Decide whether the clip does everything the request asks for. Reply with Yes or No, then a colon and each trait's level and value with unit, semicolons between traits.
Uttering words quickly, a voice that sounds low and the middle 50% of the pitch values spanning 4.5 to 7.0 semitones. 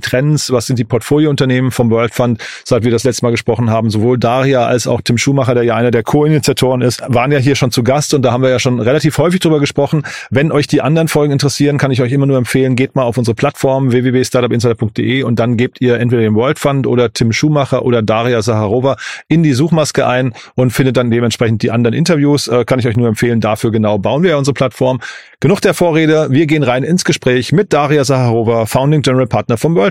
No: fast, 230 wpm; low, 130 Hz; average, 3.2 semitones